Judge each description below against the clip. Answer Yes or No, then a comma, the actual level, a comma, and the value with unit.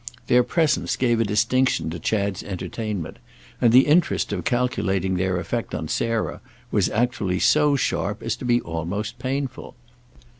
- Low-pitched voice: Yes, low, 115 Hz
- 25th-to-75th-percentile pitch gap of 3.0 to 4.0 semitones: No, average, 4.8 semitones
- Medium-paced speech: Yes, average, 150 wpm